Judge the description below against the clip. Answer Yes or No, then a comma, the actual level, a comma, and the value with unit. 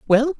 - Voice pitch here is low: No, high, 245 Hz